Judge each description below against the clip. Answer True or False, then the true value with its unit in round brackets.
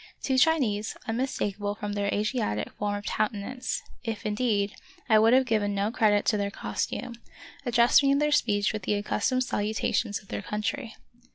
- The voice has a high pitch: True (215 Hz)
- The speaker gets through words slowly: False (170 wpm)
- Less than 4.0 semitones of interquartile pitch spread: True (3.1 semitones)